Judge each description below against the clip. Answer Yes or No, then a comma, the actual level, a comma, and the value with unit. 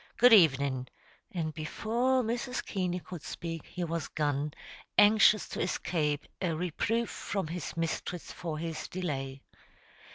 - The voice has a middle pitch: Yes, medium, 170 Hz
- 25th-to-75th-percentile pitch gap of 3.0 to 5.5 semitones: Yes, average, 5.1 semitones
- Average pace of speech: No, slow, 130 wpm